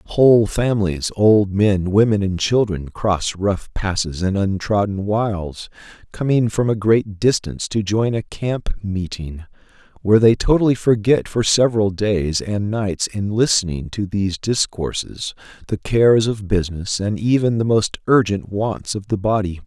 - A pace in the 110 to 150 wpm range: Yes, average, 145 wpm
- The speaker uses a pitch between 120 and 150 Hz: No, low, 105 Hz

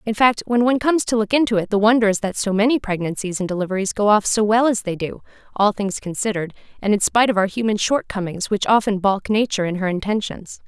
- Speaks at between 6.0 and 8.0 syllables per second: Yes, 6.5 syllables/s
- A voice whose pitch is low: No, high, 210 Hz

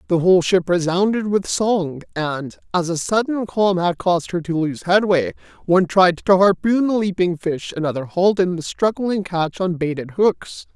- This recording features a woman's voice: No, male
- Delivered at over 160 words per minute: Yes, average, 185 wpm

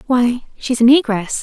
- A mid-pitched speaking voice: No, high, 245 Hz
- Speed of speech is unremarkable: Yes, average, 170 wpm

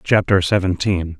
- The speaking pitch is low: Yes, very low, 90 Hz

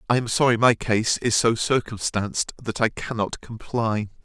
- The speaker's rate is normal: Yes, average, 170 wpm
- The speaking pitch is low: Yes, low, 110 Hz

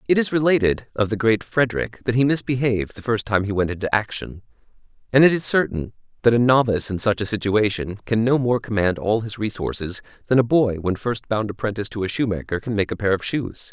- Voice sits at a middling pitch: No, low, 110 Hz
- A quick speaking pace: Yes, fast, 225 wpm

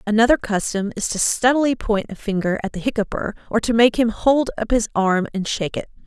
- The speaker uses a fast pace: Yes, fast, 220 wpm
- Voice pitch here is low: No, high, 220 Hz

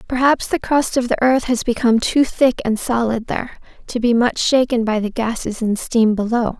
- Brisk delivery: Yes, fast, 210 wpm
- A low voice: No, high, 235 Hz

